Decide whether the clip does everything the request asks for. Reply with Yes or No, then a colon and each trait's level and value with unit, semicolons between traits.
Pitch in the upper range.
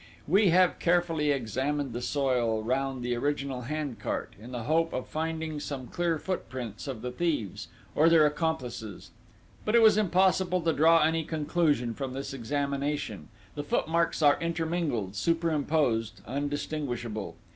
No: medium, 145 Hz